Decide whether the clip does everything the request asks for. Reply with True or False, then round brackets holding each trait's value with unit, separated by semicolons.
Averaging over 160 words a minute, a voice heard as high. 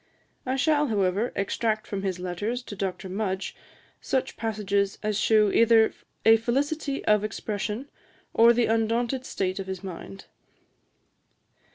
False (135 wpm; 215 Hz)